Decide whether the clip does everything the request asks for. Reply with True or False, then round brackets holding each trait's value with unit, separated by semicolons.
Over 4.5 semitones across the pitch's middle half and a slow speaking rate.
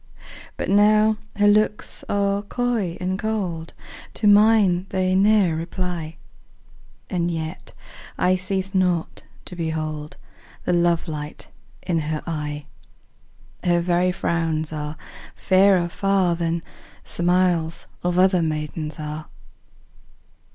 False (3.3 semitones; 115 wpm)